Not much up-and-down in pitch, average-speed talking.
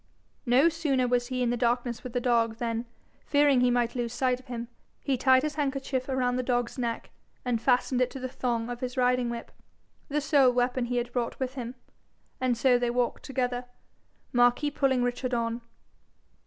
Yes: narrow, 1.3 semitones; average, 195 wpm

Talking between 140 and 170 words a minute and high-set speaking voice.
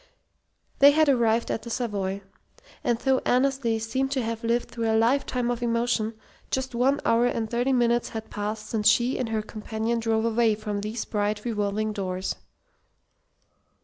Yes: average, 165 wpm; high, 230 Hz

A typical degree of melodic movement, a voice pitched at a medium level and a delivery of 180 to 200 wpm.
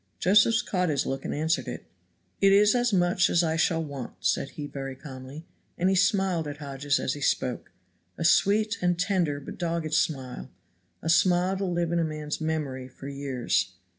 Yes: average, 4.5 semitones; medium, 160 Hz; average, 190 wpm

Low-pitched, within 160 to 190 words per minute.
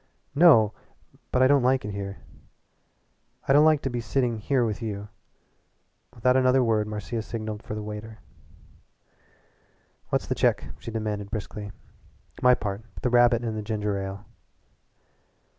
No: low, 110 Hz; average, 145 wpm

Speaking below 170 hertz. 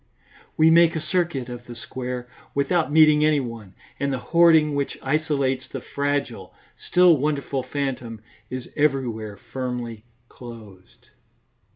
Yes: low, 135 Hz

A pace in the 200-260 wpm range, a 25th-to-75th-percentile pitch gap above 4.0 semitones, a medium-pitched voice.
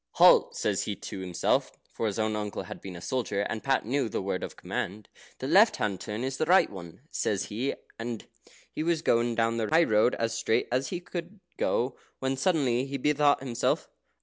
No: fast, 205 wpm; average, 4.6 semitones; low, 120 Hz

